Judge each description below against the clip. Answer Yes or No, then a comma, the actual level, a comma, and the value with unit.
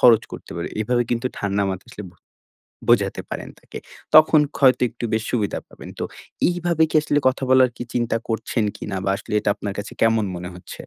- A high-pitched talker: No, low, 115 Hz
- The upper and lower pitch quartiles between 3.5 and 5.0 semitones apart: Yes, average, 4.0 semitones